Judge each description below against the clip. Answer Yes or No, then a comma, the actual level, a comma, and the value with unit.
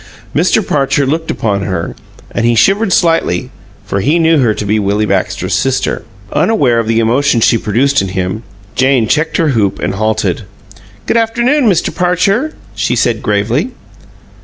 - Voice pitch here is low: Yes, low, 125 Hz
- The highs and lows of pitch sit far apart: Yes, wide, 7.6 semitones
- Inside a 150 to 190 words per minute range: Yes, average, 160 wpm